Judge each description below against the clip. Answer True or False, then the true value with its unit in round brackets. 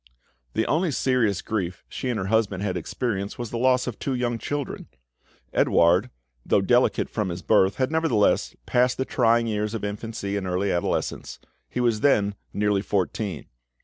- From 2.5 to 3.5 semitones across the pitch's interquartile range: False (3.9 semitones)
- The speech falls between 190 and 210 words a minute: False (170 wpm)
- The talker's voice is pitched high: False (110 Hz)